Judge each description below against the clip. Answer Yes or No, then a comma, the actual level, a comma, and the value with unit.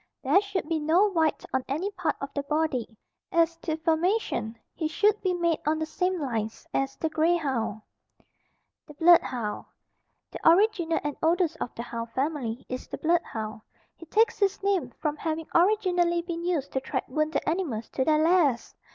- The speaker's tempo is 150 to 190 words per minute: Yes, average, 180 wpm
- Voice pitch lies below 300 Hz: No, very high, 320 Hz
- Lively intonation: No, average, 4.4 semitones